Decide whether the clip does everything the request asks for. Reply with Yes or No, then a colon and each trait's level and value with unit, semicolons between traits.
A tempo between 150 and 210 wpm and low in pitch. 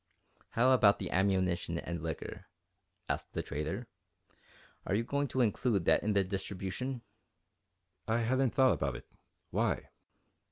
No: slow, 135 wpm; low, 100 Hz